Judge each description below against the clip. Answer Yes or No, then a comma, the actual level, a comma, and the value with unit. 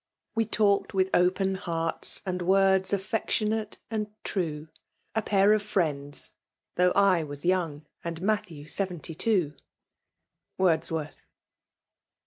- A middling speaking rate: No, slow, 115 wpm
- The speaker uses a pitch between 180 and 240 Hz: Yes, medium, 185 Hz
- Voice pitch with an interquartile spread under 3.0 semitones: No, average, 3.5 semitones